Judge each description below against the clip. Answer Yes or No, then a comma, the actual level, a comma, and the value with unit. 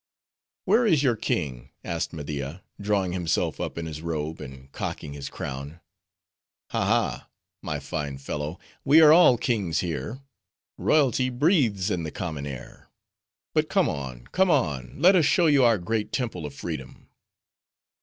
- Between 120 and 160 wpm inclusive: Yes, average, 155 wpm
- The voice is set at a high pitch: No, very low, 85 Hz